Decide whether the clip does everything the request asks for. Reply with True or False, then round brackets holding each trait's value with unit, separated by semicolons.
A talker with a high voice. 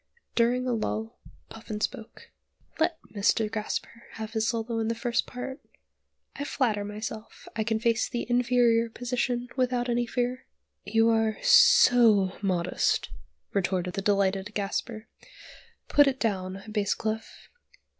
True (225 Hz)